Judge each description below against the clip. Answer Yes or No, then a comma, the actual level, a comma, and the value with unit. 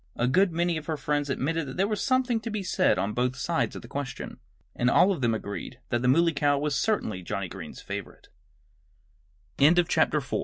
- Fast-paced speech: Yes, fast, 220 wpm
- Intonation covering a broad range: Yes, wide, 5.9 semitones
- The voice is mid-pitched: Yes, medium, 150 Hz